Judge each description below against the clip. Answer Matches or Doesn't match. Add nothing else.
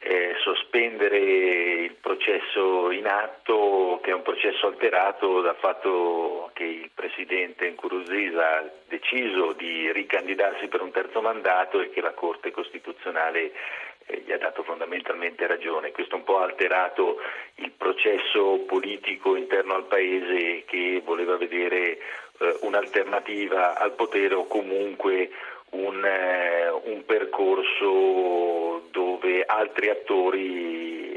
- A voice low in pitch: Doesn't match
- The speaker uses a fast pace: Doesn't match